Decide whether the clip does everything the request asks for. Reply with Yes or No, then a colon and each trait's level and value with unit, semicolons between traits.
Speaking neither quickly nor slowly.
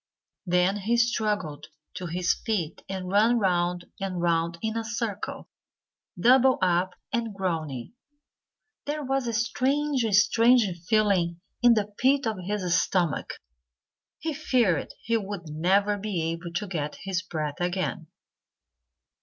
No: slow, 130 wpm